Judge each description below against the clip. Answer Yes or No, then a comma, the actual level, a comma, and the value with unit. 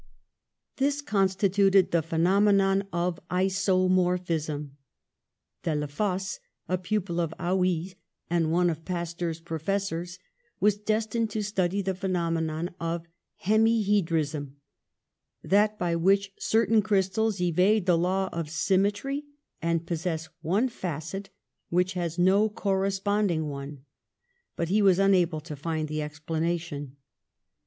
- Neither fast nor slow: No, slow, 115 wpm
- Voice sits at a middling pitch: Yes, medium, 180 Hz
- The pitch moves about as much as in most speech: Yes, average, 3.2 semitones